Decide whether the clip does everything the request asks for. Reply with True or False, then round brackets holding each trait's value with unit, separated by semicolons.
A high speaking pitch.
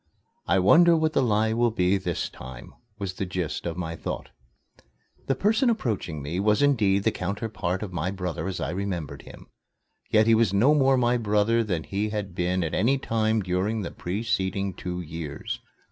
False (100 Hz)